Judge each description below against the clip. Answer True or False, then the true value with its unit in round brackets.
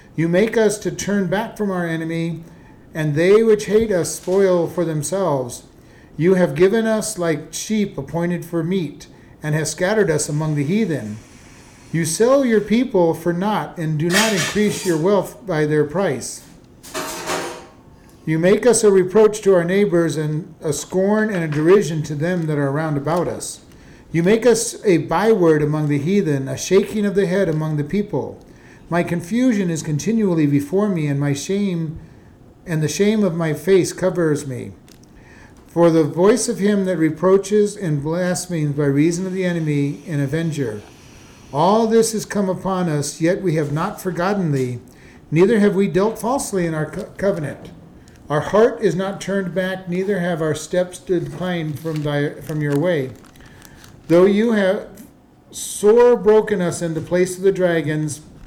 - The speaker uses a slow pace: False (170 wpm)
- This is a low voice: False (175 Hz)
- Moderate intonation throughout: True (4.3 semitones)